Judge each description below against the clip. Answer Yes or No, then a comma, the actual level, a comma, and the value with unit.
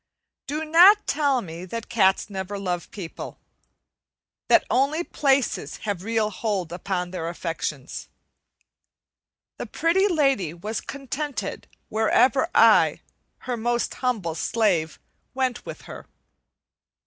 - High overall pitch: Yes, high, 225 Hz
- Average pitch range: No, wide, 7.1 semitones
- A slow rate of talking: Yes, slow, 115 wpm